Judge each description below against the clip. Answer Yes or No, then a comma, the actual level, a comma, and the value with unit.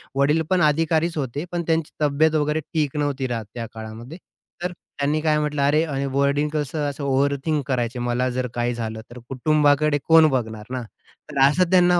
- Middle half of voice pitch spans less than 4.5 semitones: Yes, average, 3.4 semitones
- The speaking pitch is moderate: Yes, medium, 145 Hz